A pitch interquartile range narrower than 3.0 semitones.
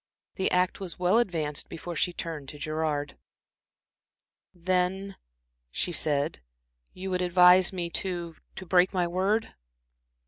Yes: narrow, 2.4 semitones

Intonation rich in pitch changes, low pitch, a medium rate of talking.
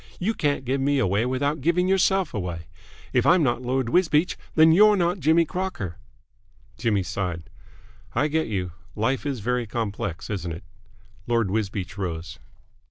Yes: wide, 8.1 semitones; low, 125 Hz; average, 155 wpm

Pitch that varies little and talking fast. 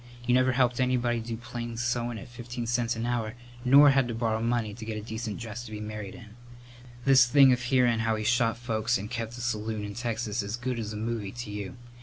Yes: narrow, 1.9 semitones; fast, 235 wpm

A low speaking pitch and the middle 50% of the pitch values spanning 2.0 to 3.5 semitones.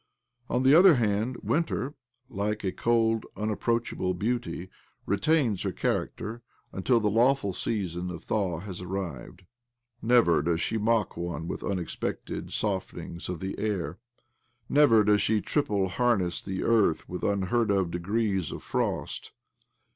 No: low, 105 Hz; average, 4.1 semitones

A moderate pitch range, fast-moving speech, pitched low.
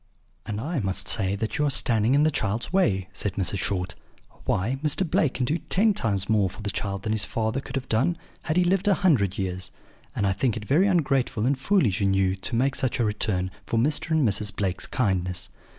No: wide, 6.7 semitones; fast, 225 wpm; low, 110 Hz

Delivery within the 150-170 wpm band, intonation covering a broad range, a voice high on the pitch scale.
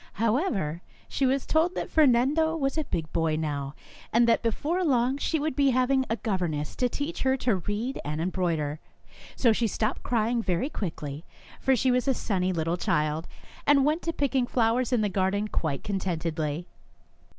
No: average, 180 wpm; wide, 7.8 semitones; high, 230 Hz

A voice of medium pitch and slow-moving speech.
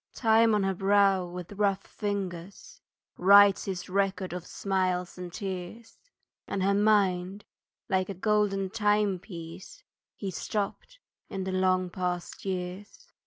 No: high, 195 Hz; slow, 125 wpm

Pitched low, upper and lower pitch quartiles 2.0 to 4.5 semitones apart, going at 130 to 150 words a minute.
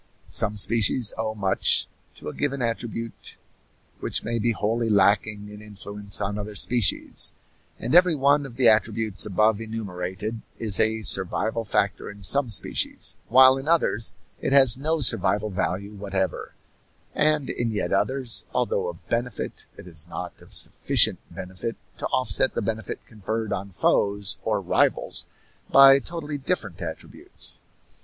Yes: low, 110 Hz; average, 3.5 semitones; average, 145 wpm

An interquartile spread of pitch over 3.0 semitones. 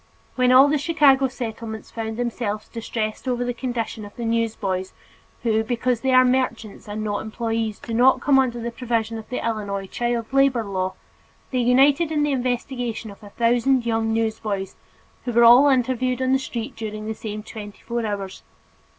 No: average, 2.7 semitones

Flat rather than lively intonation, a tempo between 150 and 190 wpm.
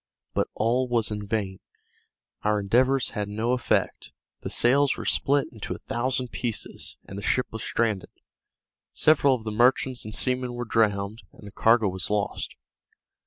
No: average, 3.3 semitones; average, 165 wpm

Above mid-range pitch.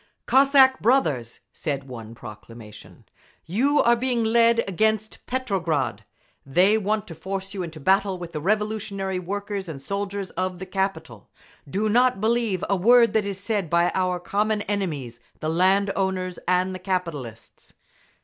Yes: high, 195 Hz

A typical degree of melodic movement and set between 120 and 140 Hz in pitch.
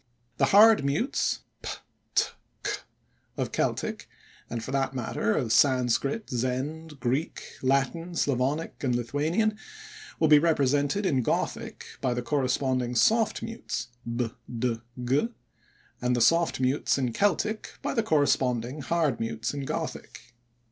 Yes: average, 4.7 semitones; low, 135 Hz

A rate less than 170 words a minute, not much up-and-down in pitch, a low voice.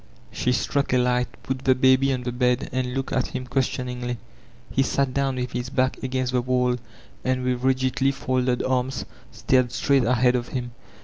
No: average, 190 wpm; narrow, 0.9 semitones; low, 130 Hz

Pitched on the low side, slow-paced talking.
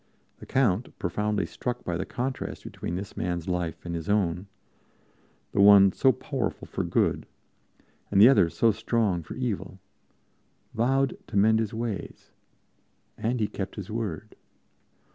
No: low, 105 Hz; average, 145 wpm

